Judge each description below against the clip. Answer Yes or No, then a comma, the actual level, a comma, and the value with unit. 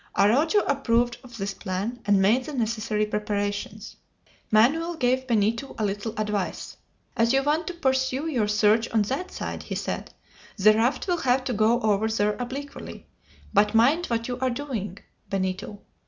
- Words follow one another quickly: No, average, 165 wpm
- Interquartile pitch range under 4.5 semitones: Yes, average, 4.0 semitones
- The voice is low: No, high, 230 Hz